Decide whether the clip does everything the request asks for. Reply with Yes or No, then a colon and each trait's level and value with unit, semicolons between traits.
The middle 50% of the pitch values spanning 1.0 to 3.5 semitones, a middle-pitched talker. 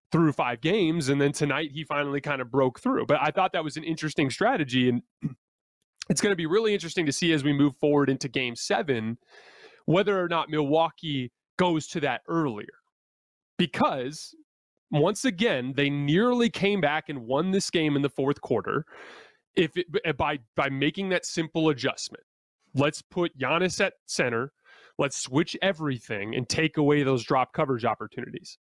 No: average, 4.2 semitones; medium, 150 Hz